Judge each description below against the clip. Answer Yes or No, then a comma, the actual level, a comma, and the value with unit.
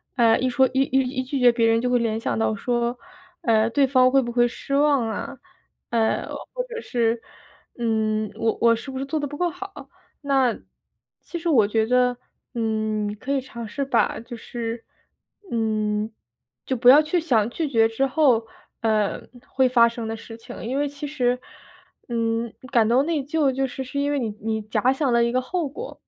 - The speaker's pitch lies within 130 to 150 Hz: No, high, 245 Hz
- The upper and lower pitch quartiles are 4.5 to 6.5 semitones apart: No, average, 3.3 semitones